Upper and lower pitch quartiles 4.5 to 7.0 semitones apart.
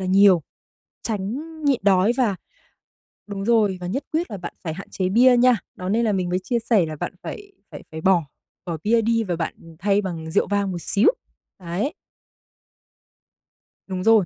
No: average, 3.9 semitones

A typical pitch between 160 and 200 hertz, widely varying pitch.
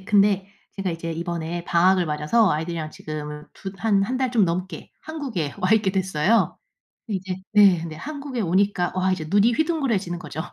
No: high, 190 Hz; average, 4.0 semitones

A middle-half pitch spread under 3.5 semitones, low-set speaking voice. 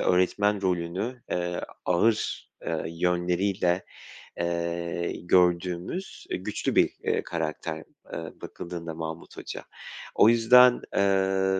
Yes: narrow, 2.4 semitones; very low, 90 Hz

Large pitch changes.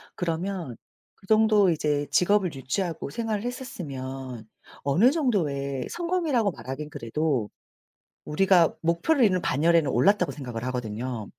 Yes: wide, 7.3 semitones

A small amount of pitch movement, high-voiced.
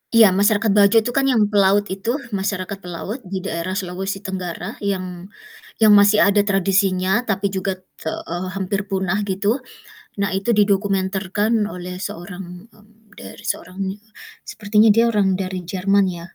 Yes: narrow, 1.8 semitones; high, 195 Hz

